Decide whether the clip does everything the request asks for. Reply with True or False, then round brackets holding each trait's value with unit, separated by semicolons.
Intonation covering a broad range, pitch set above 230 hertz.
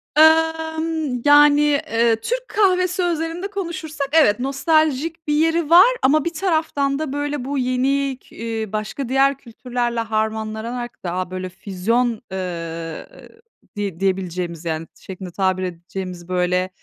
True (8.5 semitones; 255 Hz)